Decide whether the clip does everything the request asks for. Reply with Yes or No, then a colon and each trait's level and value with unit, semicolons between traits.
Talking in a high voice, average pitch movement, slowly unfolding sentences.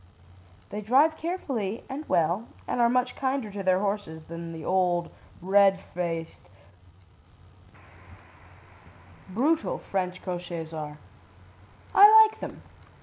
No: high, 195 Hz; wide, 6.7 semitones; slow, 110 wpm